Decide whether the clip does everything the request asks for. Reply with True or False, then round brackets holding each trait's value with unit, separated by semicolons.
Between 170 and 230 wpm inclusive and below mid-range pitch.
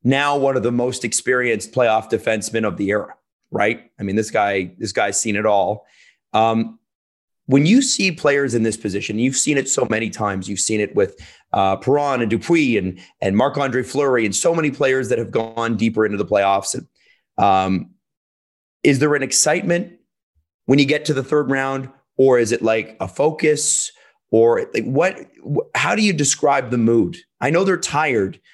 True (190 wpm; 120 Hz)